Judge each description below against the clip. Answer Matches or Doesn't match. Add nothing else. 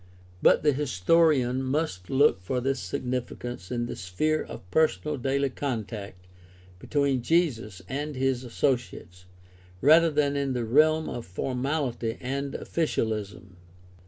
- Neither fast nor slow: Doesn't match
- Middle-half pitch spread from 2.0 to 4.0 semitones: Doesn't match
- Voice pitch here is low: Matches